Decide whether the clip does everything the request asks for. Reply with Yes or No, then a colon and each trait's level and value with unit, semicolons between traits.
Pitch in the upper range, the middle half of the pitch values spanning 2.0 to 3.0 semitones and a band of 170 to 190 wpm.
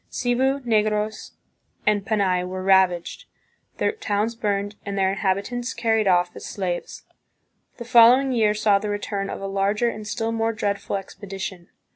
No: high, 205 Hz; narrow, 2.6 semitones; average, 150 wpm